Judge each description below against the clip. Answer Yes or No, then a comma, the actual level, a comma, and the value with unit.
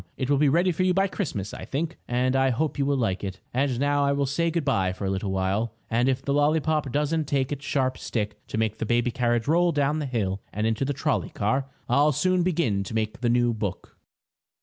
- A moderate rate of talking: No, fast, 240 wpm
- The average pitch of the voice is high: No, low, 135 Hz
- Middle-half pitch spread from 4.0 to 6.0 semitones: Yes, average, 4.7 semitones